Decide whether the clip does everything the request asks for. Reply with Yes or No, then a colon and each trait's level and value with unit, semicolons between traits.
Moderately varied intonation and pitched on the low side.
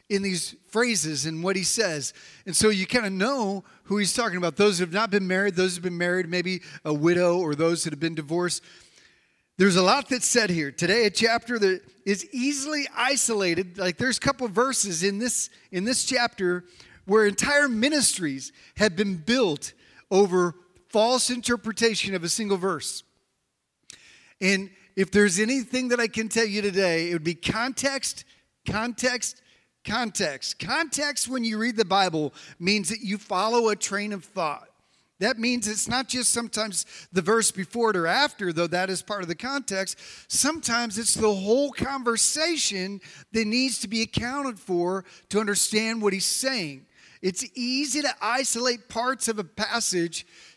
No: average, 4.5 semitones; high, 210 Hz